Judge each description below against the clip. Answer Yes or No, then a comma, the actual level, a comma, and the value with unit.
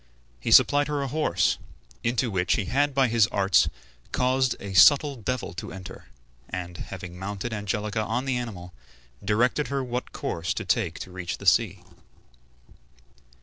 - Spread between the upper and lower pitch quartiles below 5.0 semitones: No, average, 5.3 semitones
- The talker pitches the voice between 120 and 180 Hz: No, low, 110 Hz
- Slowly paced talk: No, average, 155 wpm